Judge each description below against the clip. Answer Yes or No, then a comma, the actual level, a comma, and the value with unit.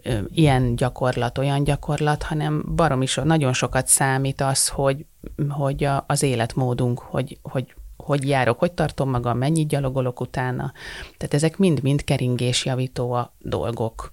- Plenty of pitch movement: No, average, 2.7 semitones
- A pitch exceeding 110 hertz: Yes, low, 135 Hz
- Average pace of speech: Yes, average, 130 wpm